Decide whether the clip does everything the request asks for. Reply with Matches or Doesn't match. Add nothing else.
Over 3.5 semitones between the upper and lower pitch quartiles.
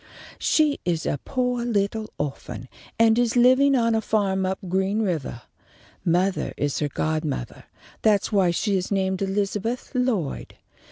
Matches